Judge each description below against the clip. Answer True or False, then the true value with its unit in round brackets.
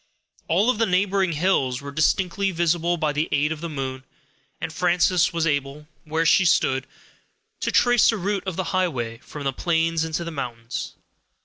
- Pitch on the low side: False (165 Hz)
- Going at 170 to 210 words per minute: True (180 wpm)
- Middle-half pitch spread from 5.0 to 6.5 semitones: False (4.1 semitones)